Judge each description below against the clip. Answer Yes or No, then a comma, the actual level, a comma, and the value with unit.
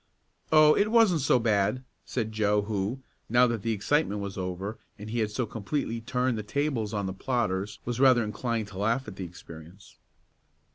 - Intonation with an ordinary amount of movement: Yes, average, 4.0 semitones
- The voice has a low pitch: Yes, low, 110 Hz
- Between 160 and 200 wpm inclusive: Yes, average, 185 wpm